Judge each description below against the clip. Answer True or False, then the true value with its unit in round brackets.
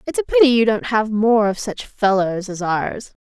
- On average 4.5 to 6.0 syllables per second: True (4.7 syllables/s)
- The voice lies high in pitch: True (210 Hz)